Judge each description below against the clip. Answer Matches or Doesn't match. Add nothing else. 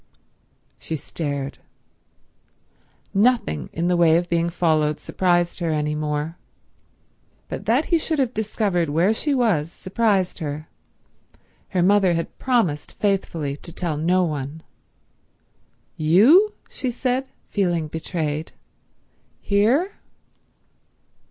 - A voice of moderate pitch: Matches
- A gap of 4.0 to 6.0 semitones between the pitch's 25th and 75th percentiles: Matches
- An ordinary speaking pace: Doesn't match